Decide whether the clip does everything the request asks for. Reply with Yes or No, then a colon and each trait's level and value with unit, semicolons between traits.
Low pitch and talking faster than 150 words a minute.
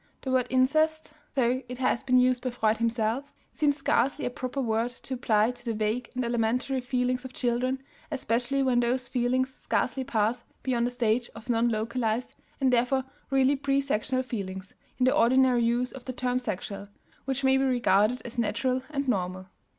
No: very high, 250 Hz; average, 180 wpm